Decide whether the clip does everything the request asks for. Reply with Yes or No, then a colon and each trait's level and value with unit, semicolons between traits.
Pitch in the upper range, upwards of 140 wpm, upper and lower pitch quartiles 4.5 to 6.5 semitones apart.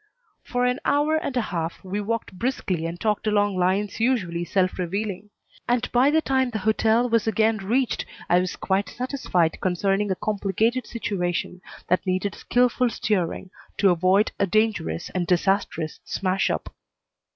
No: high, 205 Hz; average, 155 wpm; average, 4.1 semitones